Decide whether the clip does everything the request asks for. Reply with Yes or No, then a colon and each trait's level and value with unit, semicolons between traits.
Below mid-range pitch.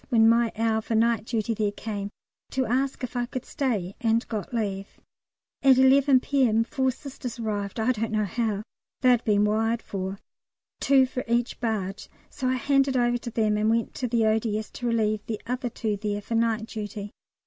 No: high, 230 Hz